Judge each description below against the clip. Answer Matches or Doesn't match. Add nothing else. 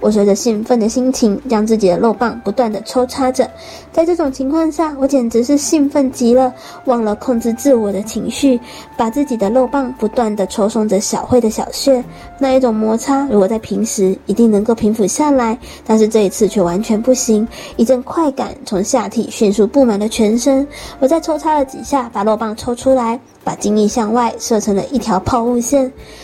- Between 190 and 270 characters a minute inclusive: Doesn't match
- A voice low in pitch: Doesn't match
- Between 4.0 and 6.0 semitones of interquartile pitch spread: Doesn't match